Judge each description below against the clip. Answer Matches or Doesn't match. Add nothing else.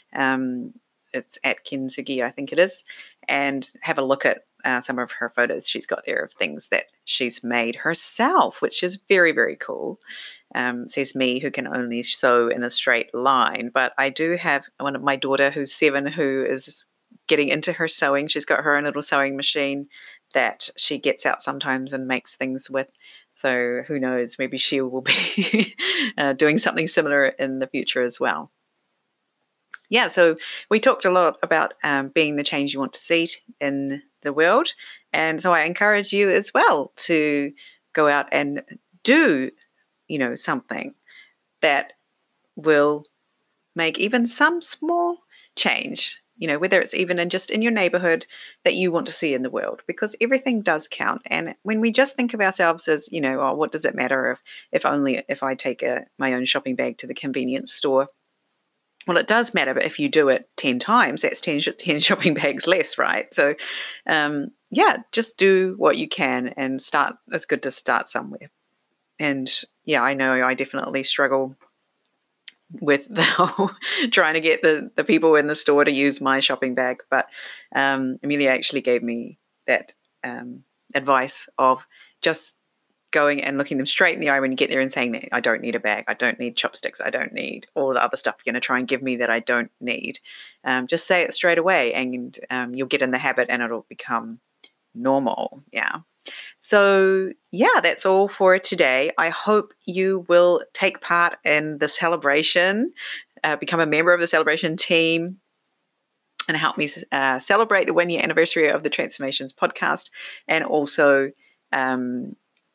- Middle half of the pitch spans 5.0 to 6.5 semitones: Matches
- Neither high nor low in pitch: Matches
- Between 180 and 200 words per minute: Matches